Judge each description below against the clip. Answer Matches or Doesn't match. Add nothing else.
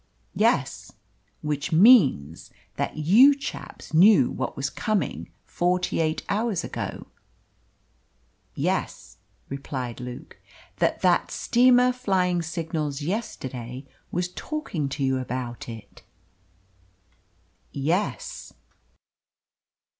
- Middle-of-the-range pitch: Matches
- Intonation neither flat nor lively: Doesn't match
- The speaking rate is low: Matches